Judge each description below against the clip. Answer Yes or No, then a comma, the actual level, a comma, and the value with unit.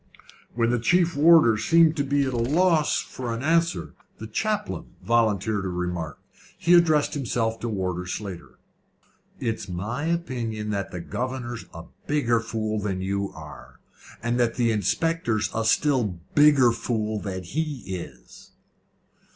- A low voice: Yes, low, 115 Hz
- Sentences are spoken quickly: No, average, 140 wpm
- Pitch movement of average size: No, wide, 6.4 semitones